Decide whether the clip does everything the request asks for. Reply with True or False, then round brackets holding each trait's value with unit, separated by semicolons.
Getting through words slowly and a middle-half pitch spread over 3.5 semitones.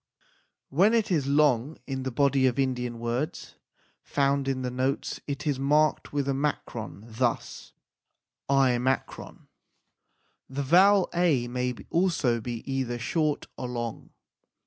False (130 wpm; 3.1 semitones)